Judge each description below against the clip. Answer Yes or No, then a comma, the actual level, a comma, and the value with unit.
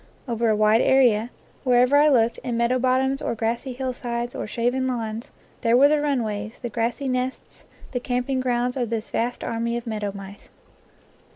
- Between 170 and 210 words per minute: Yes, average, 175 wpm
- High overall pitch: Yes, high, 240 Hz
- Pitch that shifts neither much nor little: No, narrow, 2.1 semitones